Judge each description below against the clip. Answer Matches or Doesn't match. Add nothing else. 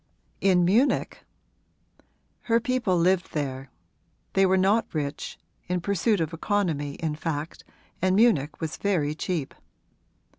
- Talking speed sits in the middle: Doesn't match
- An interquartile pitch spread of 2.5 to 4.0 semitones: Doesn't match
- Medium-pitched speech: Matches